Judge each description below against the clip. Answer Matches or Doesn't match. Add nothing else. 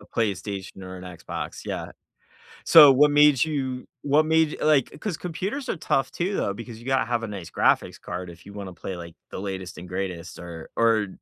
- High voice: Doesn't match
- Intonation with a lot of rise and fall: Matches